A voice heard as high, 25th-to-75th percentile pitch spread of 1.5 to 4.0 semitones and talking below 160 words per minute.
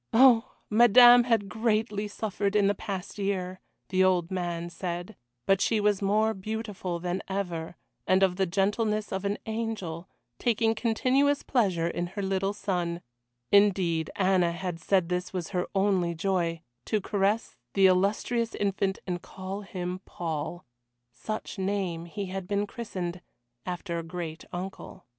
Yes: high, 195 Hz; average, 2.8 semitones; average, 150 wpm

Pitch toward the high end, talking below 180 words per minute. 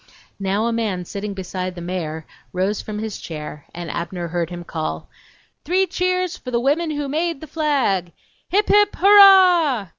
Yes: high, 215 Hz; average, 170 wpm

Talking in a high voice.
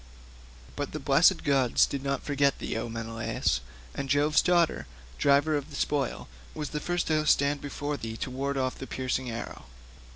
No: medium, 140 Hz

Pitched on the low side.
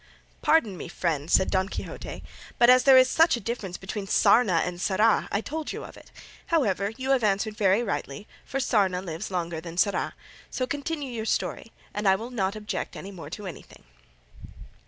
No: high, 205 Hz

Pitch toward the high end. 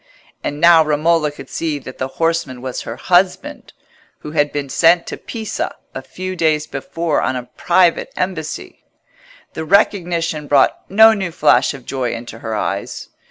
No: medium, 160 Hz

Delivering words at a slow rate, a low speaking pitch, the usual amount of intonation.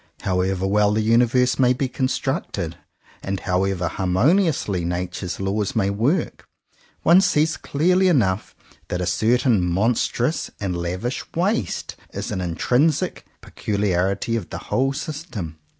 No: slow, 130 wpm; low, 105 Hz; wide, 6.4 semitones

